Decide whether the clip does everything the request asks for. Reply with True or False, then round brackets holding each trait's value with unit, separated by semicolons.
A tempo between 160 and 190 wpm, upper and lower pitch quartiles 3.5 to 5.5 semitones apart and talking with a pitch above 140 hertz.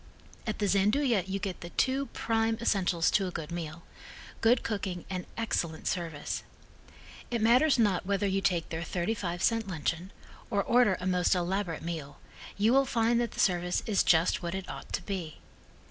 True (180 wpm; 4.4 semitones; 190 Hz)